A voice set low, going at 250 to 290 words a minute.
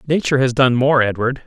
No: low, 130 Hz; fast, 205 wpm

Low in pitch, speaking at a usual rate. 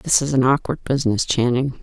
Yes: low, 130 Hz; average, 195 wpm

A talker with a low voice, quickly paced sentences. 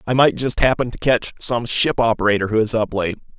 Yes: low, 115 Hz; fast, 230 wpm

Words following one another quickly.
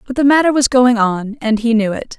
Yes: fast, 275 wpm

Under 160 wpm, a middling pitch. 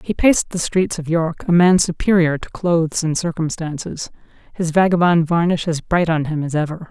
No: average, 185 wpm; medium, 165 Hz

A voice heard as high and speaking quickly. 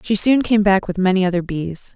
Yes: high, 195 Hz; fast, 245 wpm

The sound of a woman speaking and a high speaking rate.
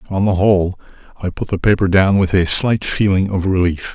No: male; fast, 215 wpm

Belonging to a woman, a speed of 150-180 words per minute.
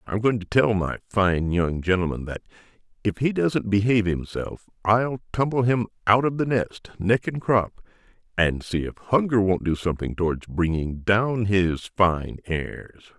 No: male; average, 170 wpm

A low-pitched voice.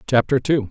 Yes: low, 125 Hz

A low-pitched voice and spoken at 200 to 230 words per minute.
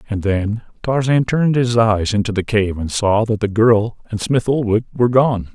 Yes: low, 110 Hz; fast, 205 wpm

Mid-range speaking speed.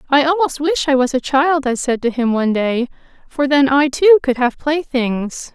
No: fast, 215 wpm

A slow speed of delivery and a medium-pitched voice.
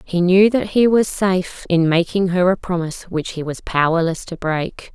No: fast, 205 wpm; medium, 180 Hz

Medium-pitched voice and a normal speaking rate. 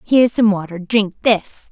No: high, 205 Hz; average, 175 wpm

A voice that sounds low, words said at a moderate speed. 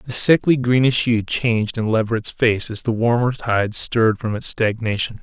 Yes: low, 115 Hz; average, 185 wpm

